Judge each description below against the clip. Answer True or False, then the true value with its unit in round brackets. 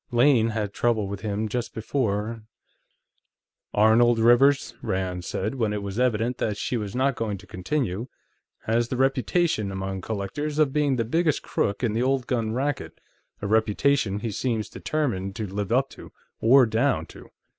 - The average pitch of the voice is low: True (115 Hz)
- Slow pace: False (170 wpm)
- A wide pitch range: False (3.9 semitones)